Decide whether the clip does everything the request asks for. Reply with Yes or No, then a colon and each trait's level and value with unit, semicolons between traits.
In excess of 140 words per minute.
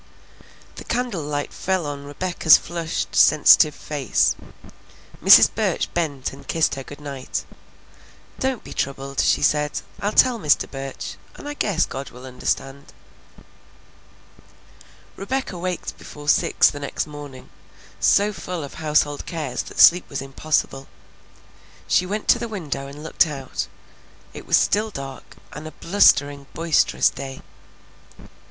No: slow, 135 wpm